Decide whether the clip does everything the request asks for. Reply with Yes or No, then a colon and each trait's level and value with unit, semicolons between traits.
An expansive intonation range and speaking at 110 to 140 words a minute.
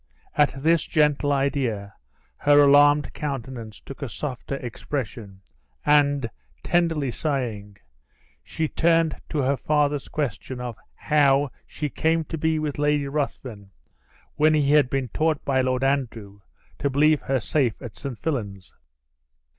No: average, 3.1 semitones; slow, 135 wpm